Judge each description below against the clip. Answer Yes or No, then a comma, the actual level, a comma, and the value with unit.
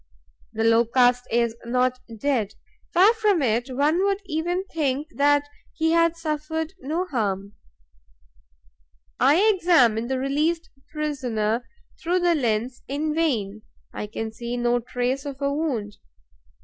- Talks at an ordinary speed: No, slow, 130 wpm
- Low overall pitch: No, very high, 275 Hz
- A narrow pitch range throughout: No, wide, 5.4 semitones